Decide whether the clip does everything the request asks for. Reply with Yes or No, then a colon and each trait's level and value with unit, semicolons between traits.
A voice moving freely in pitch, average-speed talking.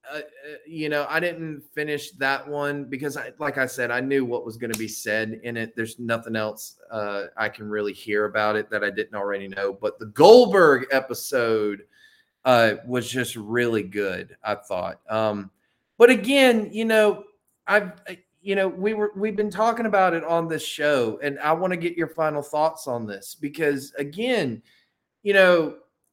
Yes: wide, 8.5 semitones; average, 185 wpm